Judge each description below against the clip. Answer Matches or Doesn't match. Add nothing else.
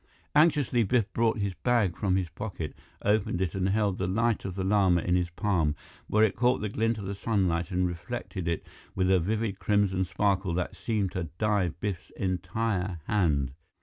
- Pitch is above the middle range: Doesn't match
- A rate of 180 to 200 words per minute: Matches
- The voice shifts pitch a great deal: Doesn't match